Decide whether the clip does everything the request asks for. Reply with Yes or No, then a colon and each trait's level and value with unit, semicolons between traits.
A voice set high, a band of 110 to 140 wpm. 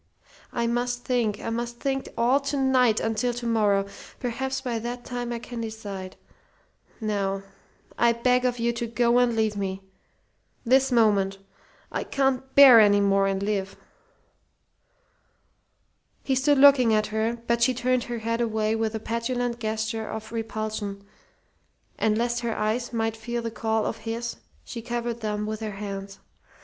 No: high, 230 Hz; average, 160 wpm